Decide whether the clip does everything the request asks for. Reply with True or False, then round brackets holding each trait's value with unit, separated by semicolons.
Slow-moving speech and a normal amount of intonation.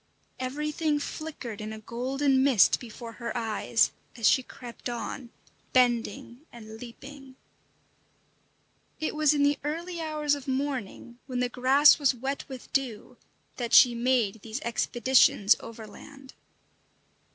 True (130 wpm; 3.4 semitones)